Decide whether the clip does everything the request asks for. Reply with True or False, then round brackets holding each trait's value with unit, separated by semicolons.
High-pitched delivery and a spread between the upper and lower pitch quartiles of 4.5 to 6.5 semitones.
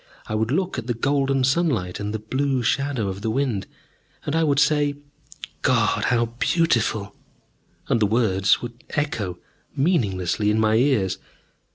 False (120 Hz; 5.1 semitones)